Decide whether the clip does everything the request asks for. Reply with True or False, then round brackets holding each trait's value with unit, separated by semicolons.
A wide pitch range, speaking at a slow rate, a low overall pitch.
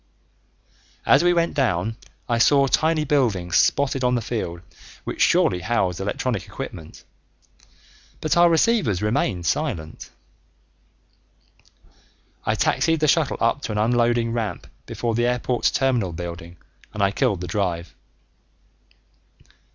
True (6.8 semitones; 125 wpm; 115 Hz)